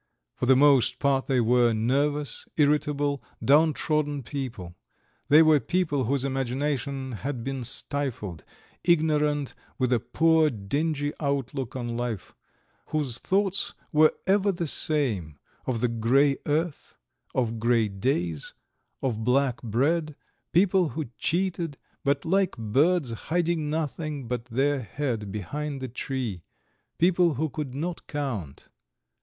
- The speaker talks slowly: Yes, slow, 125 wpm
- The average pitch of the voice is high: No, medium, 140 Hz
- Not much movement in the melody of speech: No, average, 4.0 semitones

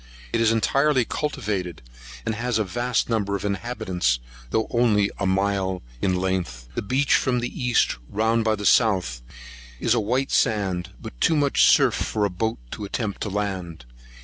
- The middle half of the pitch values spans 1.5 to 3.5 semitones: No, average, 4.0 semitones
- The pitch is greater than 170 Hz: No, low, 105 Hz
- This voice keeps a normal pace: Yes, average, 170 wpm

